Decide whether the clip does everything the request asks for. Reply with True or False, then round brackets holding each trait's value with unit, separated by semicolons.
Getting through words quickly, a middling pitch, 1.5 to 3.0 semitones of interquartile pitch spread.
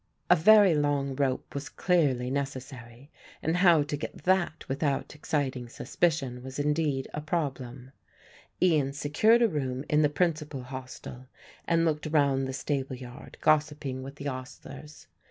False (145 wpm; 145 Hz; 2.7 semitones)